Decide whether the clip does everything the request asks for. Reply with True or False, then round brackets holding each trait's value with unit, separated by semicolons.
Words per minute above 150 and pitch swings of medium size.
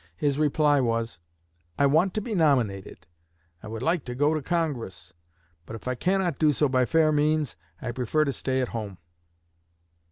True (180 wpm; 4.5 semitones)